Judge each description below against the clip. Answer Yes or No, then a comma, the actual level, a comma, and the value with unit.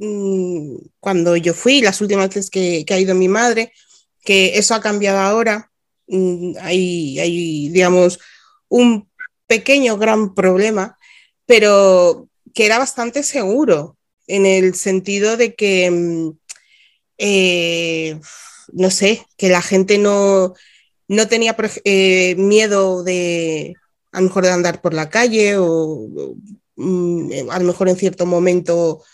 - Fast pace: No, average, 130 wpm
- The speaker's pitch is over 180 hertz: Yes, high, 190 Hz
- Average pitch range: Yes, average, 3.3 semitones